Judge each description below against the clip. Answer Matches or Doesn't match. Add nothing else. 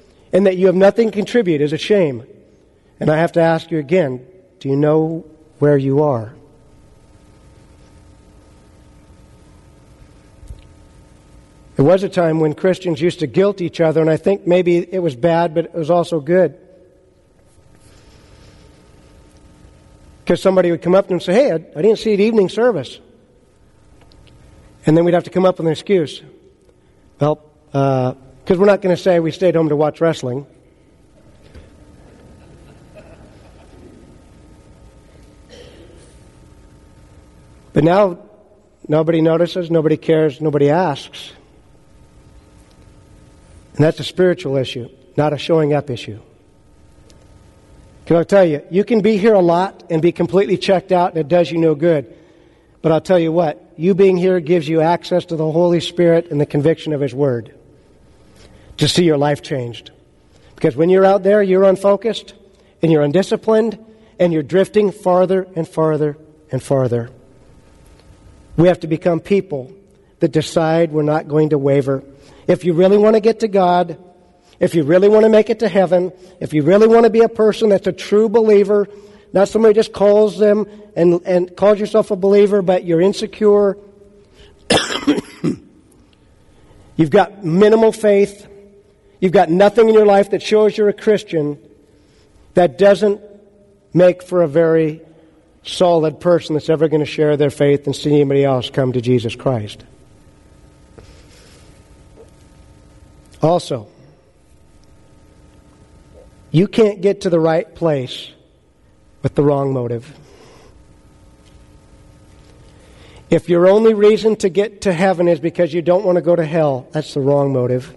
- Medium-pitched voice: Matches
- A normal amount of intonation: Matches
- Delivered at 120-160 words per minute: Matches